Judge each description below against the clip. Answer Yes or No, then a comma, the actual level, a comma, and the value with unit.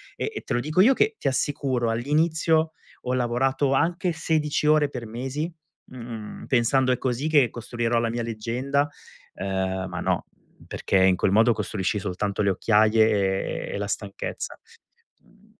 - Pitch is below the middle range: Yes, low, 120 Hz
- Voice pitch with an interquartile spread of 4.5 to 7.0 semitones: Yes, average, 5.0 semitones